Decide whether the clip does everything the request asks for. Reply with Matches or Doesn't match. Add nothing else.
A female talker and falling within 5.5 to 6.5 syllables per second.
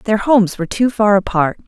Matches